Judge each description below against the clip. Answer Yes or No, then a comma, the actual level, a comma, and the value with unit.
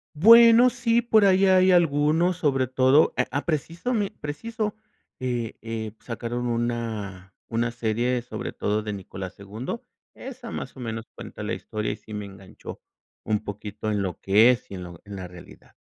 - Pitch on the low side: Yes, low, 120 Hz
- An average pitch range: No, wide, 8.6 semitones